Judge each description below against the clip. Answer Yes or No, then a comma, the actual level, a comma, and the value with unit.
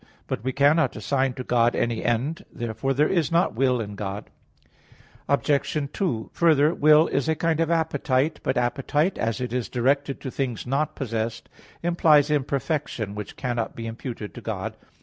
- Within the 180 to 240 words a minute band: No, average, 170 wpm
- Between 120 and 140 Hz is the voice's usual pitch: Yes, low, 135 Hz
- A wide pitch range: No, average, 4.2 semitones